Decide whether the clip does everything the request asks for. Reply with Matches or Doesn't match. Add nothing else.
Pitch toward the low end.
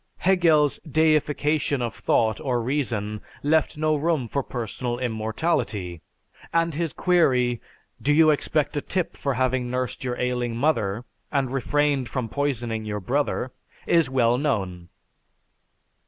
Matches